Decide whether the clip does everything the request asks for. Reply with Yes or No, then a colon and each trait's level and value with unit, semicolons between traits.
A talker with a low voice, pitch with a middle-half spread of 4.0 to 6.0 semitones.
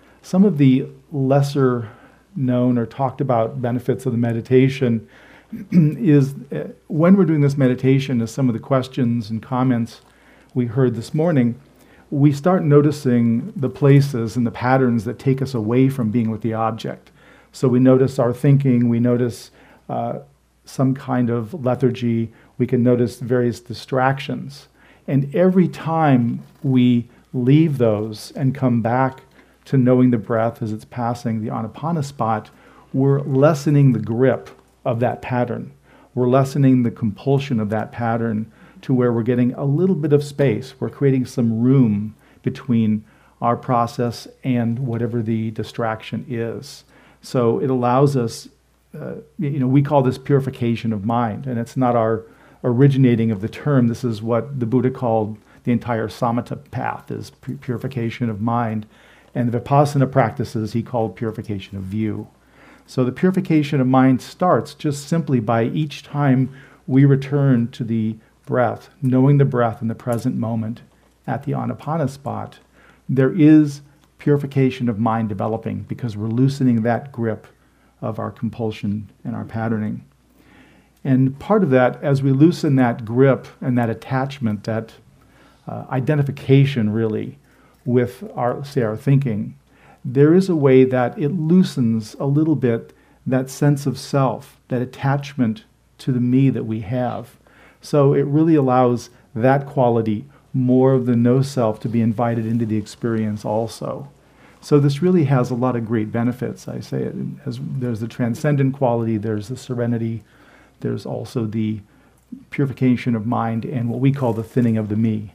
No: low, 125 Hz; average, 3.0 semitones